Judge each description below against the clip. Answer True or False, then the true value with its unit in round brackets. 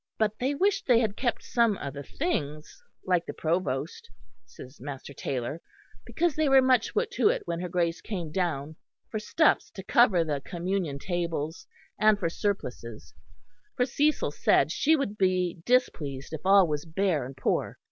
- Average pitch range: False (7.7 semitones)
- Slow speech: False (170 wpm)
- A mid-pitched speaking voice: True (180 Hz)